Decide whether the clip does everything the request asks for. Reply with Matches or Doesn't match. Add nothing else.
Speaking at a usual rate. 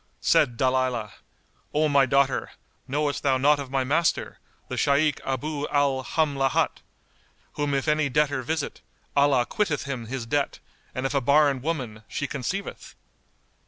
Matches